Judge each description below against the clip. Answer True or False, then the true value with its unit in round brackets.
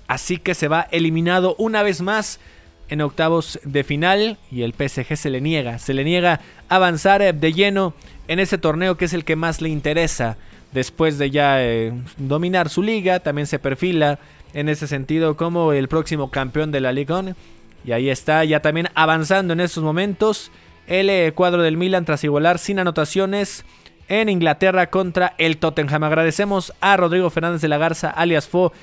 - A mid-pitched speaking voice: True (160 Hz)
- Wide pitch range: False (3.7 semitones)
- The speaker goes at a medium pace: True (180 wpm)